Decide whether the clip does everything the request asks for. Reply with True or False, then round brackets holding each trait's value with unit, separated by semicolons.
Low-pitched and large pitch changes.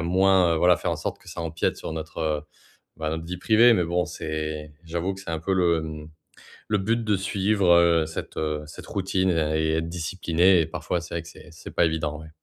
False (85 Hz; 2.8 semitones)